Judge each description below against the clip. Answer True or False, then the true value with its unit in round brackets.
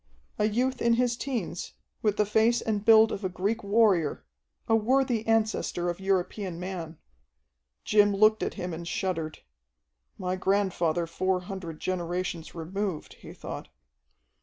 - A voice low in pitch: False (195 Hz)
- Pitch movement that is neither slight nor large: True (3.7 semitones)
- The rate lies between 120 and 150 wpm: True (140 wpm)